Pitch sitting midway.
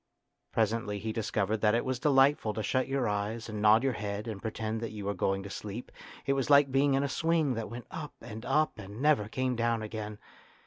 No: low, 115 Hz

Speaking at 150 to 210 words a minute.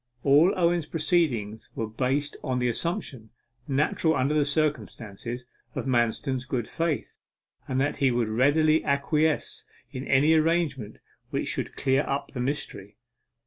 No: average, 140 wpm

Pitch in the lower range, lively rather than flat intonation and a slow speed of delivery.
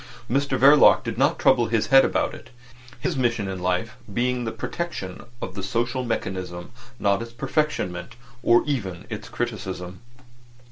No: low, 115 Hz; wide, 5.7 semitones; average, 150 wpm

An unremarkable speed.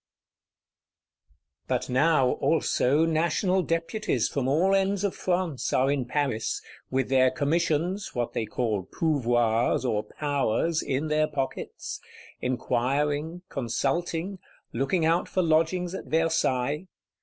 No: slow, 115 wpm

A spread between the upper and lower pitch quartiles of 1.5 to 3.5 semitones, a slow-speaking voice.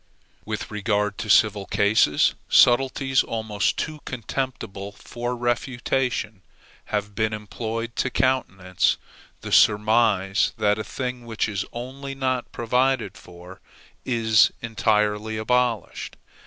Yes: average, 3.1 semitones; slow, 110 wpm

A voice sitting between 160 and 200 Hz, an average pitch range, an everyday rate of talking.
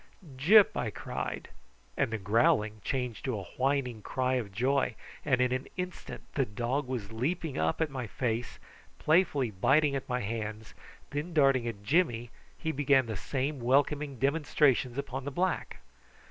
No: low, 130 Hz; average, 3.8 semitones; average, 160 wpm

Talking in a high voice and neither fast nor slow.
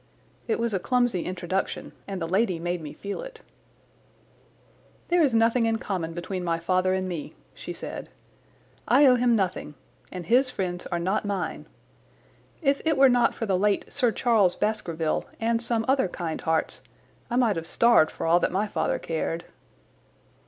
Yes: high, 200 Hz; average, 175 wpm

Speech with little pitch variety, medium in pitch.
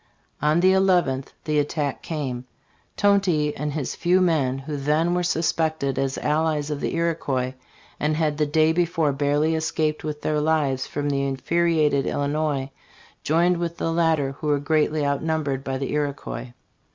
Yes: narrow, 2.3 semitones; medium, 150 Hz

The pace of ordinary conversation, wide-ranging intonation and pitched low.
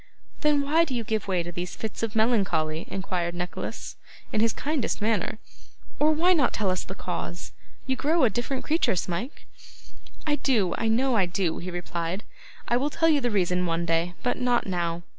No: average, 195 wpm; wide, 6.9 semitones; high, 215 Hz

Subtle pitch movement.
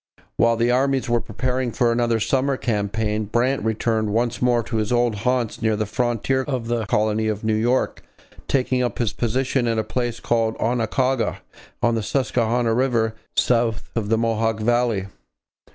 Yes: narrow, 2.0 semitones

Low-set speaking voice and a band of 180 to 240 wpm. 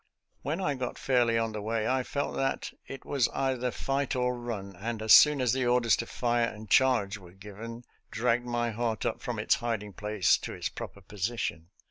Yes: low, 120 Hz; average, 200 wpm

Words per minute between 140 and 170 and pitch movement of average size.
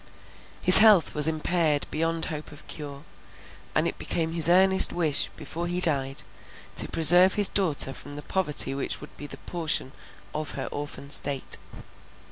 Yes: average, 160 wpm; average, 3.3 semitones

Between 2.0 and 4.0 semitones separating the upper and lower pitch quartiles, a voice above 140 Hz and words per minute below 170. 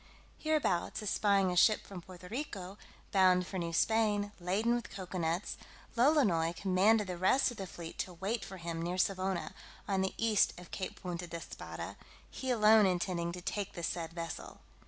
No: average, 3.3 semitones; high, 190 Hz; average, 175 wpm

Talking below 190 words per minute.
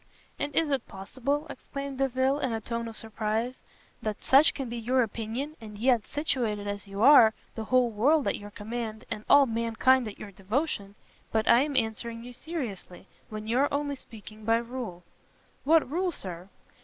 Yes: average, 180 wpm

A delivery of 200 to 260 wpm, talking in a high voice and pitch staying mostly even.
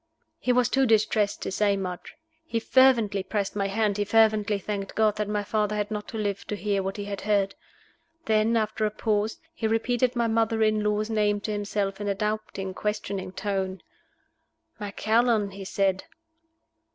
No: average, 175 wpm; high, 210 Hz; narrow, 1.7 semitones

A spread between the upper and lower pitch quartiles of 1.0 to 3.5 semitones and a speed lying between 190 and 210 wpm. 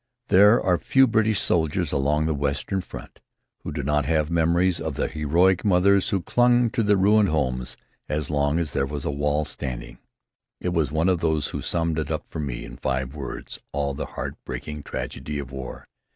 No: average, 4.5 semitones; average, 195 wpm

